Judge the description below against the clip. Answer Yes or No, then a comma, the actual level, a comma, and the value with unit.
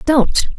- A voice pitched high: Yes, very high, 280 Hz